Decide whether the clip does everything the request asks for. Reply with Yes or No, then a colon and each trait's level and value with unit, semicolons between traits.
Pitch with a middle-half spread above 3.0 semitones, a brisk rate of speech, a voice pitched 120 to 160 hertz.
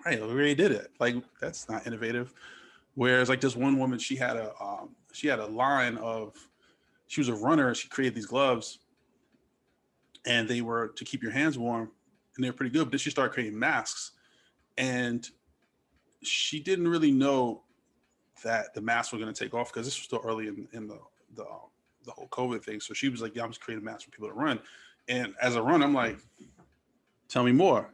No: narrow, 2.6 semitones; fast, 210 wpm; low, 125 Hz